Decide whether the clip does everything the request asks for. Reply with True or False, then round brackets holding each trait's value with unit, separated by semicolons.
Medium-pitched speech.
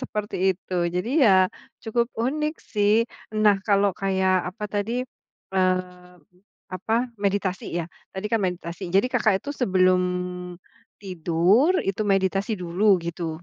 False (195 Hz)